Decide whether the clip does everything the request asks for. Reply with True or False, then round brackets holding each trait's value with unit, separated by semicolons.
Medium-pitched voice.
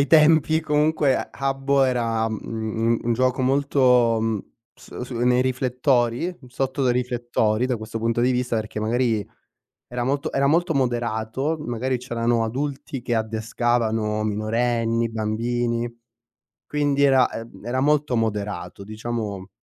False (120 Hz)